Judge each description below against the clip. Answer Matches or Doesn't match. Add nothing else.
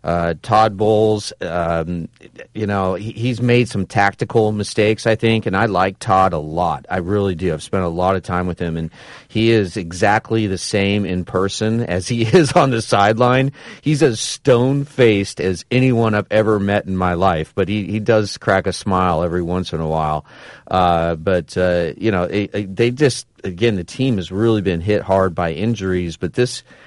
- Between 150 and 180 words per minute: Doesn't match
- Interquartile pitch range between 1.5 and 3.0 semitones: Doesn't match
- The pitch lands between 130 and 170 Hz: Doesn't match